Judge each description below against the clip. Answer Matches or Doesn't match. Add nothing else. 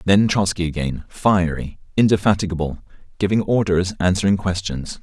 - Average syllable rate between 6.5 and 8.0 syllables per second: Doesn't match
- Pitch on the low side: Matches